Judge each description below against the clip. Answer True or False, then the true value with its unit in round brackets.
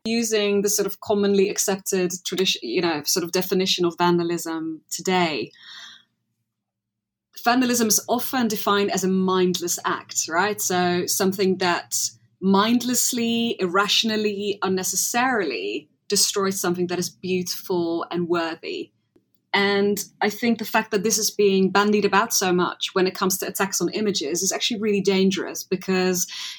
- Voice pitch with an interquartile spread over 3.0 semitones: False (2.7 semitones)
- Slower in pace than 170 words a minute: True (140 wpm)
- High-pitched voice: True (195 Hz)